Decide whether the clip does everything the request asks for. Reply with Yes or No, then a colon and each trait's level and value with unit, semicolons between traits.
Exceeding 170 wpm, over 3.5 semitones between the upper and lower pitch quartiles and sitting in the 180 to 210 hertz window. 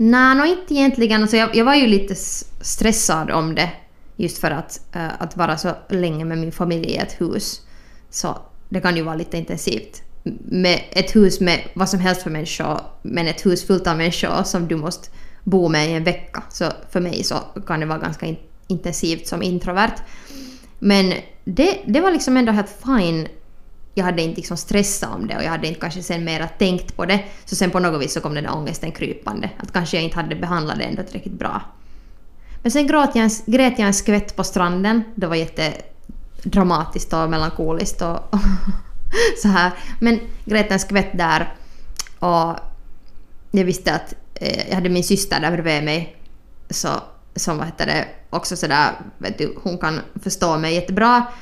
Yes: average, 190 wpm; average, 3.9 semitones; medium, 185 Hz